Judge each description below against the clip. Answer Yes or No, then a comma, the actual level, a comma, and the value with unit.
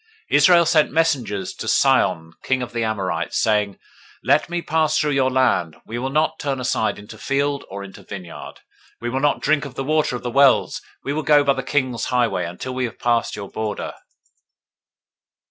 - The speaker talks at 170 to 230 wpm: Yes, average, 195 wpm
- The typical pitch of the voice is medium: No, low, 130 Hz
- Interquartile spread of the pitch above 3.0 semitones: Yes, average, 5.3 semitones